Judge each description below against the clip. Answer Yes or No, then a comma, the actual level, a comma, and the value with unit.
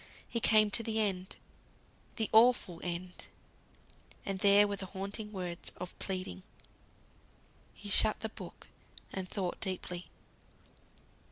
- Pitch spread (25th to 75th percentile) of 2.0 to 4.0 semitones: Yes, narrow, 2.6 semitones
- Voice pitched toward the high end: Yes, high, 195 Hz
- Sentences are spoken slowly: Yes, slow, 120 wpm